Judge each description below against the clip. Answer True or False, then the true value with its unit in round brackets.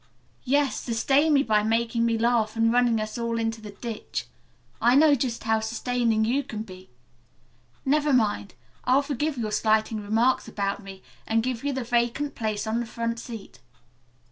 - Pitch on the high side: True (230 Hz)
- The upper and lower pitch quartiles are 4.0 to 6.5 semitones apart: False (2.5 semitones)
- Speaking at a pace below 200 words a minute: True (170 wpm)